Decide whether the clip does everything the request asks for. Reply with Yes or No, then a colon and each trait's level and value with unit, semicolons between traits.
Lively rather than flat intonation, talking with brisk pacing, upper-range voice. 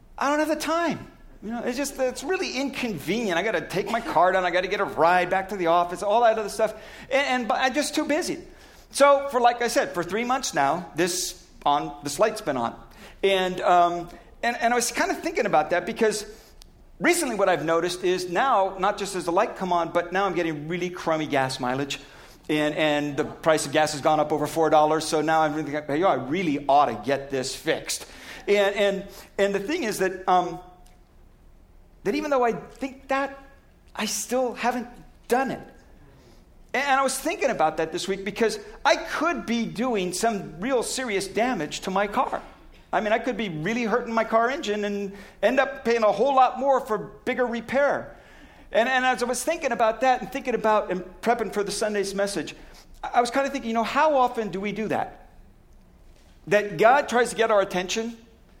Yes: wide, 5.9 semitones; fast, 215 wpm; high, 210 Hz